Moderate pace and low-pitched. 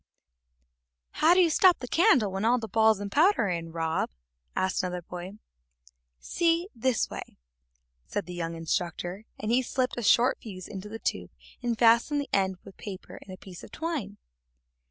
No: average, 180 wpm; high, 215 Hz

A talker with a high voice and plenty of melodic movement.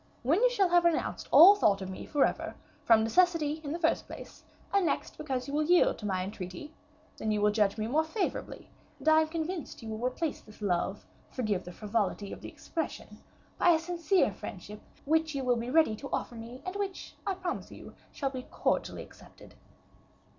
Yes: very high, 280 Hz; wide, 7.5 semitones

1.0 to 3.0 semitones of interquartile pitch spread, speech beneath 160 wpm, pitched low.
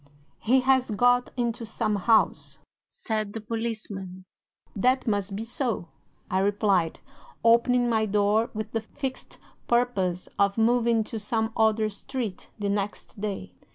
No: average, 2.7 semitones; slow, 135 wpm; high, 220 Hz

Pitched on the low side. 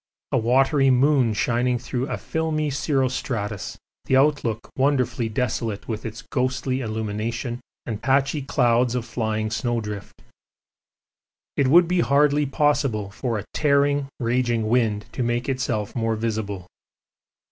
Yes: low, 125 Hz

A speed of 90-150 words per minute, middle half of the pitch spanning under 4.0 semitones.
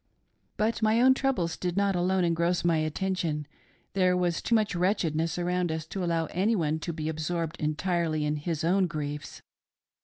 No: average, 165 wpm; average, 3.1 semitones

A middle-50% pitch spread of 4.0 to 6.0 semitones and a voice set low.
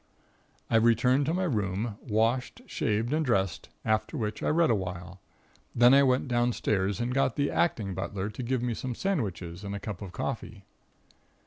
Yes: average, 4.3 semitones; low, 115 Hz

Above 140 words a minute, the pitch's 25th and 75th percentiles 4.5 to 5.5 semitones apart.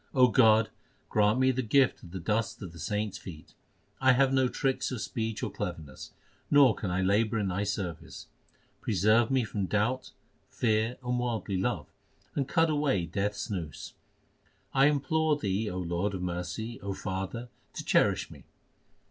Yes: average, 165 wpm; average, 5.1 semitones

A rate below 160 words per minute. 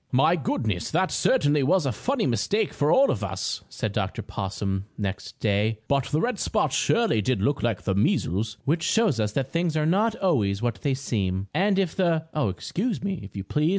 No: fast, 205 wpm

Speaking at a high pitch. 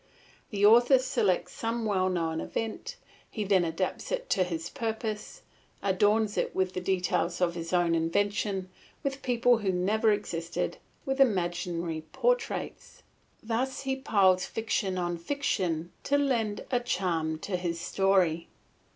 Yes: high, 195 Hz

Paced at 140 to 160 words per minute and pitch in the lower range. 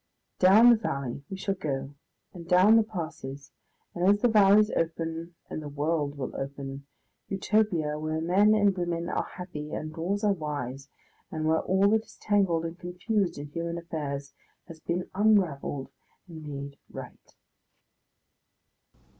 No: average, 145 wpm; medium, 170 Hz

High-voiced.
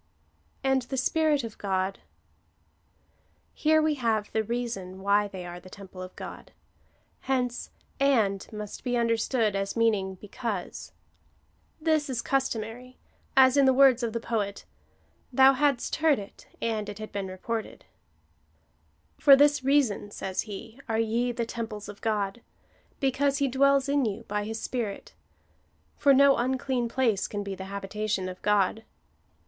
Yes: high, 225 Hz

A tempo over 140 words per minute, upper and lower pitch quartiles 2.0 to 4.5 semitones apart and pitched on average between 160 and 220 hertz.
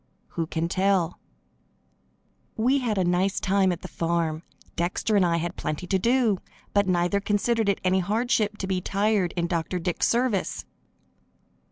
Yes: average, 160 wpm; average, 3.2 semitones; high, 190 Hz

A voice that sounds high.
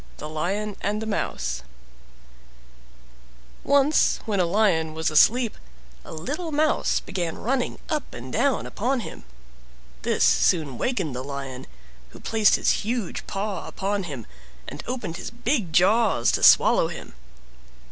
Yes: high, 200 Hz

